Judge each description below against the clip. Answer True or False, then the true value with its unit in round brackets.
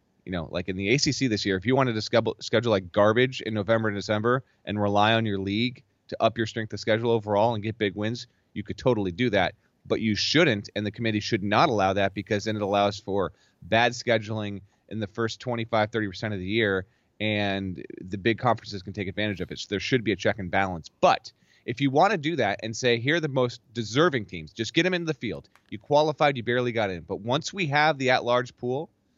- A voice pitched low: True (110 Hz)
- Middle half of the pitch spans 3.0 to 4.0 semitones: True (3.4 semitones)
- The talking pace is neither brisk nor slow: False (245 wpm)